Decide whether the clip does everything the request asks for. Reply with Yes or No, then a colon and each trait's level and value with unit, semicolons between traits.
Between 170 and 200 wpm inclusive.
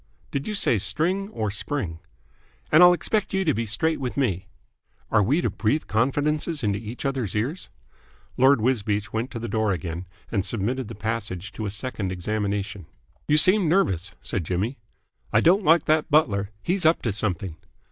Yes: average, 175 wpm